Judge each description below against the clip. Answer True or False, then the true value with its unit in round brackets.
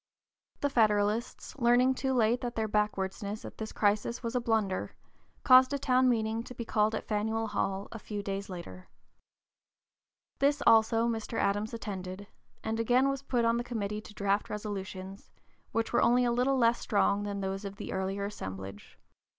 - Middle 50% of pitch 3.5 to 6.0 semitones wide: False (3.0 semitones)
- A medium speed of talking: True (180 wpm)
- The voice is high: True (220 Hz)